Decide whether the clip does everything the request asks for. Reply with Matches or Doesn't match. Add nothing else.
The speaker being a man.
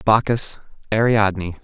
Matches